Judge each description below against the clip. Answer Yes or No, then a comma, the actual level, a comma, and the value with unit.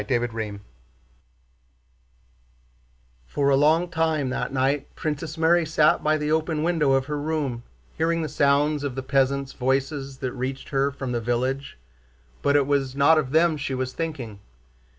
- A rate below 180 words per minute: Yes, average, 160 wpm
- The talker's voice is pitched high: No, medium, 140 Hz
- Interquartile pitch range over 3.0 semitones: No, average, 2.7 semitones